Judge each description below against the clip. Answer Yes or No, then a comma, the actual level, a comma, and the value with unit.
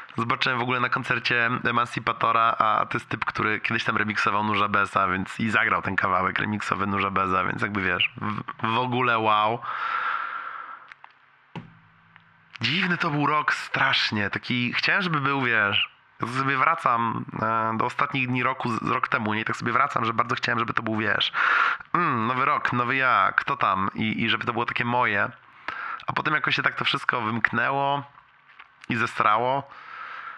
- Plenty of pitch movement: No, average, 3.3 semitones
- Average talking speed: No, fast, 170 wpm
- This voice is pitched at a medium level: No, low, 115 Hz